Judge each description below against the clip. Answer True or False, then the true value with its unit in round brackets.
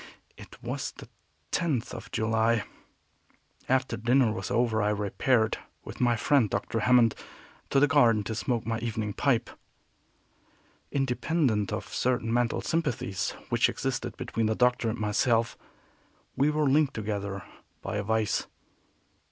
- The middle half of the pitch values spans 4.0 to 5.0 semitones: False (2.8 semitones)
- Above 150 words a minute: False (135 wpm)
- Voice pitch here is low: True (115 Hz)